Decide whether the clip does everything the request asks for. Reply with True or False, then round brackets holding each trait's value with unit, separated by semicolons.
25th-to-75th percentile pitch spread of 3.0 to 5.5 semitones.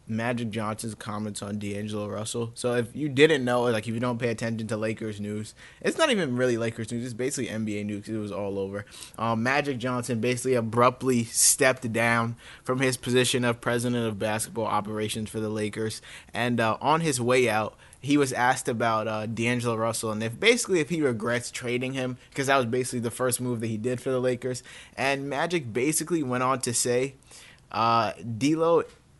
False (2.4 semitones)